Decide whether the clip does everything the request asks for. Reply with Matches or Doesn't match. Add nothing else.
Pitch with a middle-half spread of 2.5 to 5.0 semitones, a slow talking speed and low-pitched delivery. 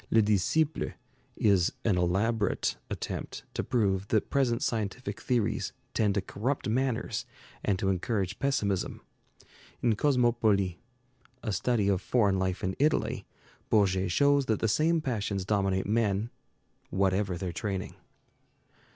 Matches